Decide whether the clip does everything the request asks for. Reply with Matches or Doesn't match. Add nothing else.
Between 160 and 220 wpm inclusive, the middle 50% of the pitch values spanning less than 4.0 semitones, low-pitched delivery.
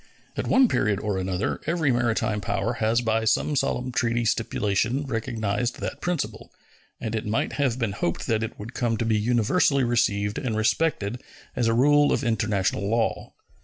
Matches